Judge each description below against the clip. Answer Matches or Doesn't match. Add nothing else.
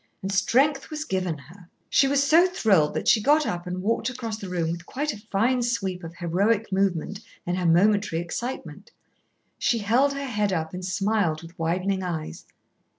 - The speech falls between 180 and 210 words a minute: Matches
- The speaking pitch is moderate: Doesn't match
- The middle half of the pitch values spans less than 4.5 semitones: Doesn't match